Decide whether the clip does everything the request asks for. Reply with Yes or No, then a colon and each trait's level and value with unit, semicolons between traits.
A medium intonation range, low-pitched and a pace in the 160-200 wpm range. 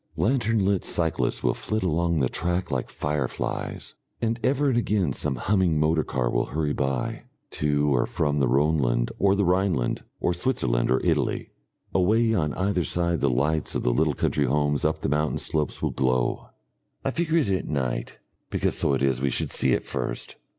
No: wide, 6.1 semitones; very low, 80 Hz; average, 185 wpm